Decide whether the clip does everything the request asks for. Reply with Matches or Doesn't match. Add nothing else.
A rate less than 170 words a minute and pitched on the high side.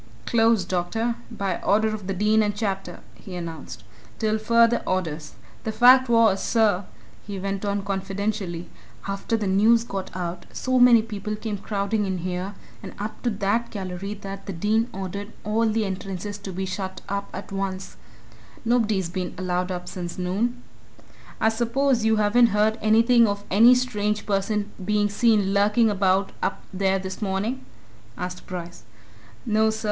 Matches